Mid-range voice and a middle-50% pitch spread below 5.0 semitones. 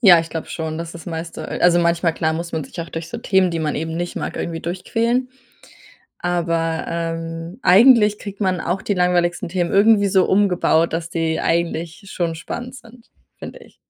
Yes: medium, 175 Hz; average, 2.7 semitones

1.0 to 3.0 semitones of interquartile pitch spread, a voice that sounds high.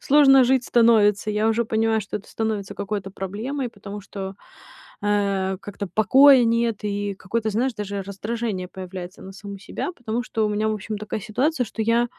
Yes: narrow, 2.6 semitones; high, 215 Hz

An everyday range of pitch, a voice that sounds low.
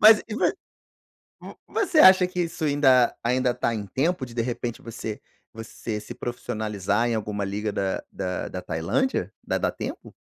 No: wide, 6.3 semitones; low, 120 Hz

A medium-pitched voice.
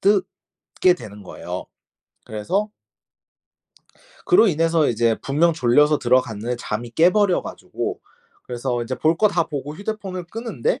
Yes: medium, 155 Hz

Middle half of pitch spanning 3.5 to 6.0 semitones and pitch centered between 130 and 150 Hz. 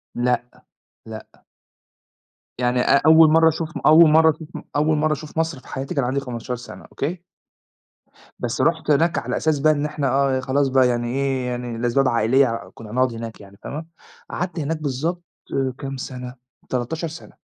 Yes: average, 4.0 semitones; low, 135 Hz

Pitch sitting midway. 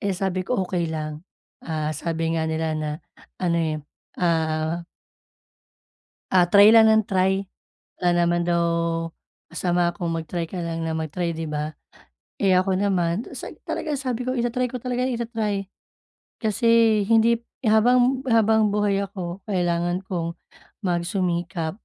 Yes: medium, 180 Hz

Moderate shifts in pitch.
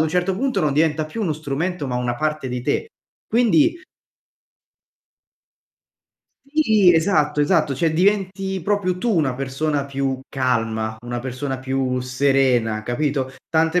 No: wide, 5.7 semitones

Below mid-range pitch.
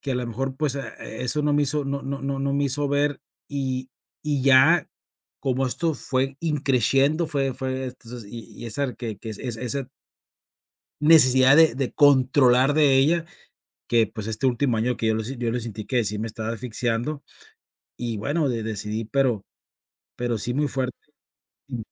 Yes: low, 130 Hz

